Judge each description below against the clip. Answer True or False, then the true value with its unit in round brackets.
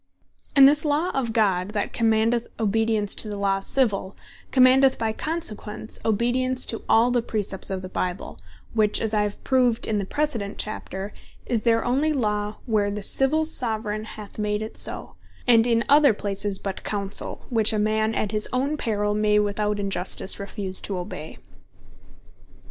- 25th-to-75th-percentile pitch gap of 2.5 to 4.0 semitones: True (3.0 semitones)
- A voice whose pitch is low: False (215 Hz)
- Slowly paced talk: False (165 wpm)